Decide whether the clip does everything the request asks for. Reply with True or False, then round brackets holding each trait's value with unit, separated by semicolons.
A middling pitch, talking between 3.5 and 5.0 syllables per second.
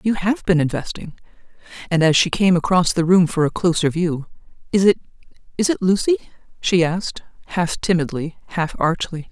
False (175 Hz; 5.4 syllables/s)